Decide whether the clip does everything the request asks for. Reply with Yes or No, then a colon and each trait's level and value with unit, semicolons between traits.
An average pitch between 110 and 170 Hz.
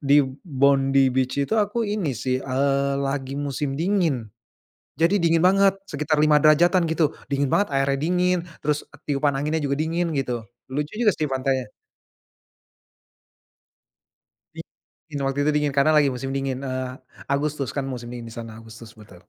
Yes: medium, 140 Hz